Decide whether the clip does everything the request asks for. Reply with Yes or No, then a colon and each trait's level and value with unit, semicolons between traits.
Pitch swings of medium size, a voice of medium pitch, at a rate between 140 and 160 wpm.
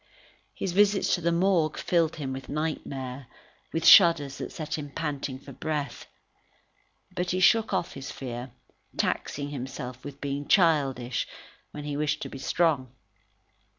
Yes: average, 3.8 semitones; medium, 145 Hz; average, 150 wpm